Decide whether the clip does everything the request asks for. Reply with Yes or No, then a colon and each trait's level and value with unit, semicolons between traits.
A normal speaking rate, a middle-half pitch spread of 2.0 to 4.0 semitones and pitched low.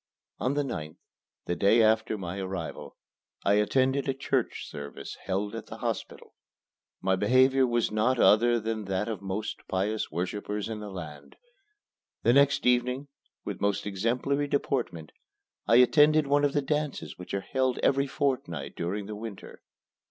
No: average, 160 wpm; average, 5.3 semitones; low, 110 Hz